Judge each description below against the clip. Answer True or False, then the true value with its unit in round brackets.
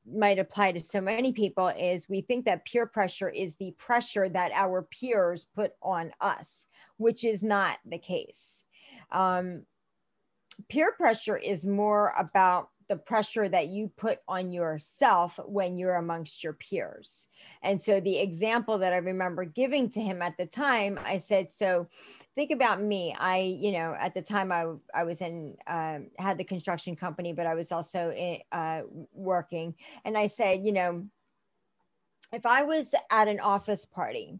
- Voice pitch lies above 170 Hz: True (190 Hz)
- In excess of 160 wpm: True (170 wpm)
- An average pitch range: True (3.0 semitones)